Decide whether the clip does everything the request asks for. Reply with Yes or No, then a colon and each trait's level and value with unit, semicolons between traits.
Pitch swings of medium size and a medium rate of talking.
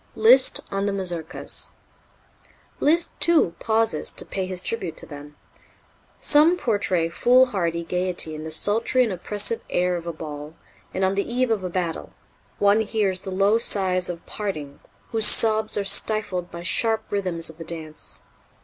Yes: average, 4.5 semitones; average, 160 wpm